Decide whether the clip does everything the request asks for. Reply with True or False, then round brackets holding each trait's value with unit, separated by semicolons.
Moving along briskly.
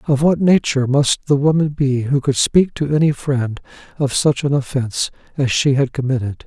False (195 wpm)